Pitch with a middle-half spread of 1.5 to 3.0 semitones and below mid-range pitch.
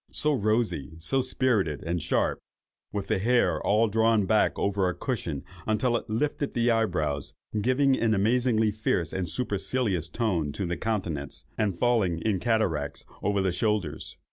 No: average, 4.9 semitones; low, 105 Hz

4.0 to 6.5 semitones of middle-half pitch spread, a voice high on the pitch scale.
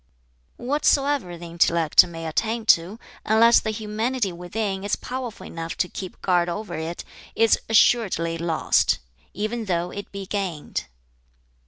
Yes: average, 4.7 semitones; high, 195 Hz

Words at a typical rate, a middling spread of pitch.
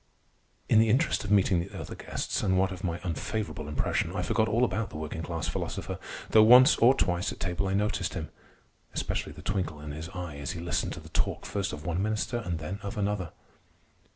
No: fast, 210 wpm; average, 3.9 semitones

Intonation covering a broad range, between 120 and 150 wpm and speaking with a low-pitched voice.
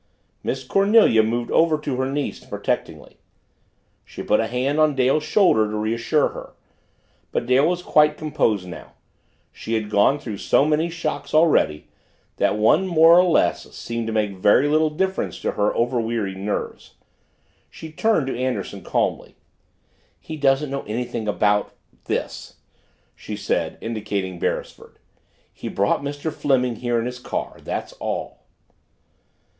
Yes: wide, 5.8 semitones; average, 145 wpm; low, 130 Hz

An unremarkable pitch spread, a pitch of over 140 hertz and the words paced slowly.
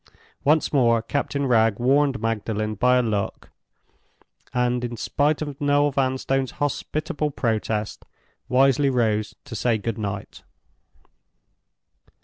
No: average, 4.0 semitones; low, 125 Hz; slow, 115 wpm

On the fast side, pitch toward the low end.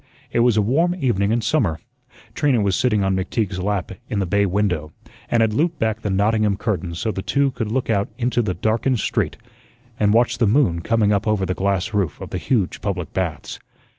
Yes: fast, 210 wpm; low, 105 Hz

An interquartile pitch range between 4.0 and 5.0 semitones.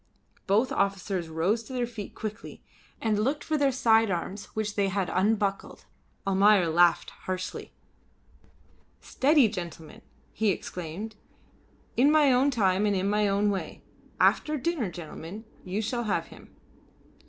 No: average, 3.6 semitones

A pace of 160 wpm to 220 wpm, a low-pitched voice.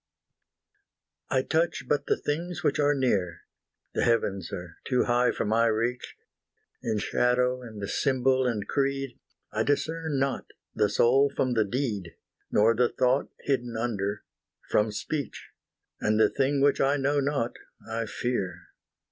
No: average, 145 wpm; low, 125 Hz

